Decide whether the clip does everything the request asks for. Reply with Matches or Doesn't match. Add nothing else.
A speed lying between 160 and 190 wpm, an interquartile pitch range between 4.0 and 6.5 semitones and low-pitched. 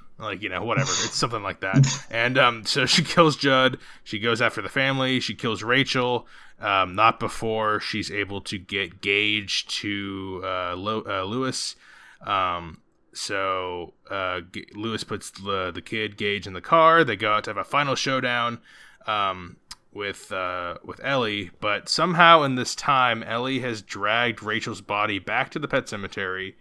Matches